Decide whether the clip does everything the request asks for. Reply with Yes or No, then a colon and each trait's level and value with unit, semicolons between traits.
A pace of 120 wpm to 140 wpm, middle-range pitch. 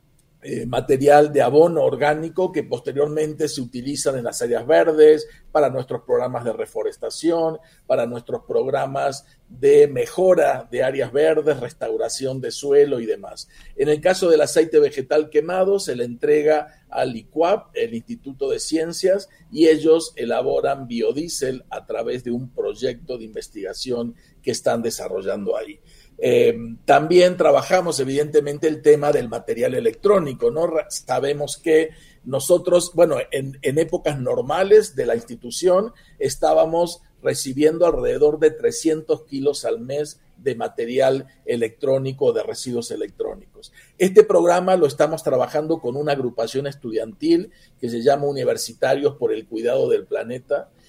Yes: average, 135 wpm; medium, 165 Hz